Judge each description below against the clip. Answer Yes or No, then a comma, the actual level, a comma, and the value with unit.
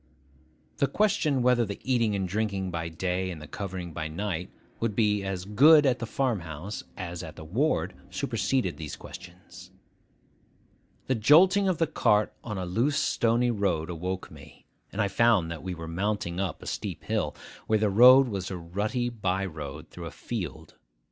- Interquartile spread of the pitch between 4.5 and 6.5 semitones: Yes, average, 5.1 semitones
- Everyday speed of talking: Yes, average, 175 wpm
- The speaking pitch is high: No, low, 100 Hz